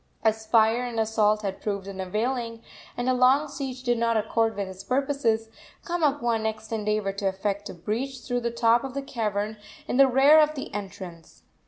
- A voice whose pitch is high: Yes, high, 225 Hz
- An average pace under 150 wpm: No, average, 185 wpm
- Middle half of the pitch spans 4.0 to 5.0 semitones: No, average, 3.5 semitones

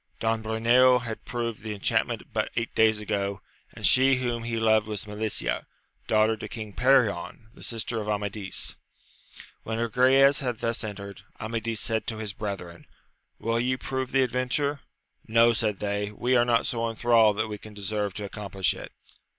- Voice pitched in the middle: No, low, 110 Hz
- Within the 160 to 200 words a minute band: Yes, average, 175 wpm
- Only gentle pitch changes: Yes, narrow, 2.2 semitones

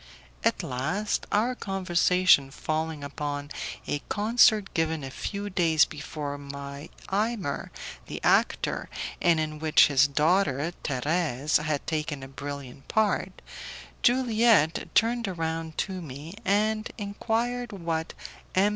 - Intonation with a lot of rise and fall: Yes, wide, 6.0 semitones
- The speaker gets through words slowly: Yes, slow, 120 wpm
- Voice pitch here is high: No, medium, 160 Hz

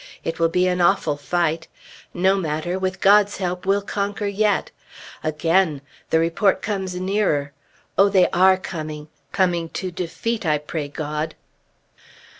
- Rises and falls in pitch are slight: No, average, 3.5 semitones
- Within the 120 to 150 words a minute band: Yes, average, 140 wpm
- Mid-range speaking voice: Yes, medium, 180 Hz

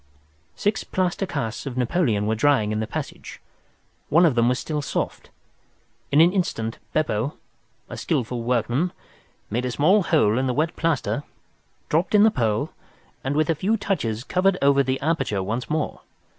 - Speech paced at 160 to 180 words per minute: Yes, average, 170 wpm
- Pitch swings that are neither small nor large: No, wide, 6.2 semitones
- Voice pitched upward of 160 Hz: No, medium, 140 Hz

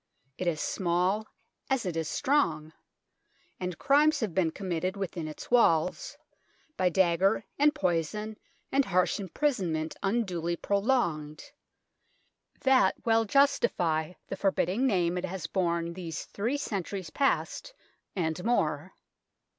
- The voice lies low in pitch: No, medium, 185 Hz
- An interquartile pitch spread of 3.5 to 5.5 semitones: Yes, average, 5.0 semitones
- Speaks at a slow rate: Yes, slow, 120 wpm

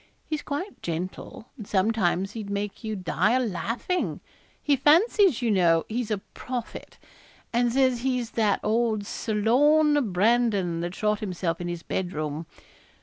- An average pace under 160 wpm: Yes, average, 150 wpm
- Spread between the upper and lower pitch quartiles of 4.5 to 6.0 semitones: Yes, average, 5.0 semitones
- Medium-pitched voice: No, high, 220 Hz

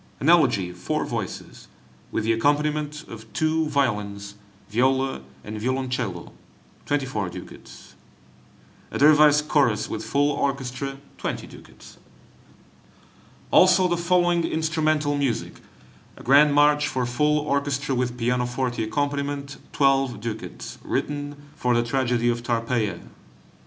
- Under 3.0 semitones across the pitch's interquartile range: No, average, 3.6 semitones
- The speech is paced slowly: Yes, slow, 115 wpm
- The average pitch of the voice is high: No, low, 135 Hz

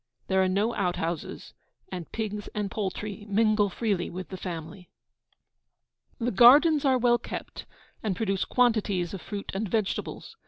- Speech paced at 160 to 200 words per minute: No, average, 150 wpm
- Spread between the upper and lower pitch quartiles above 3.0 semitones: Yes, average, 3.4 semitones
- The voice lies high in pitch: Yes, high, 205 Hz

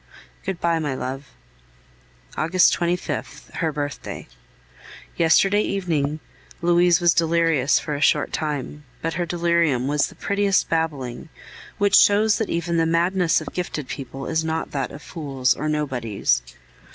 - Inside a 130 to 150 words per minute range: Yes, average, 140 wpm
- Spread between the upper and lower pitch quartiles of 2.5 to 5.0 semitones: Yes, average, 3.2 semitones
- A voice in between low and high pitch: Yes, medium, 160 Hz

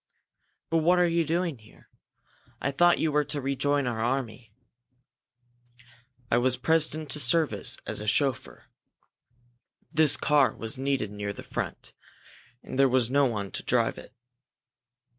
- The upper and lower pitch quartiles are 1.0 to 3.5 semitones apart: No, average, 4.4 semitones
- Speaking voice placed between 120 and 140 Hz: Yes, low, 135 Hz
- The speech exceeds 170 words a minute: No, average, 150 wpm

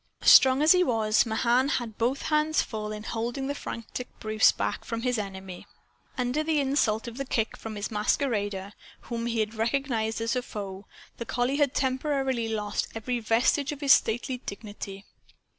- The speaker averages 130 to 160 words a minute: No, average, 175 wpm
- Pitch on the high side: Yes, high, 235 Hz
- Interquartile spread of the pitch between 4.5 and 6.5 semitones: No, average, 3.6 semitones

